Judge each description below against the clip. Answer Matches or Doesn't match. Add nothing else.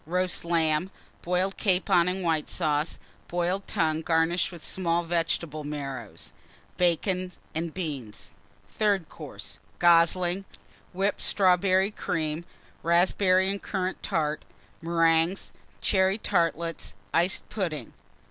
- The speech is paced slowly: Matches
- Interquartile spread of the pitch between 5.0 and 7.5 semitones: Doesn't match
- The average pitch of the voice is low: Doesn't match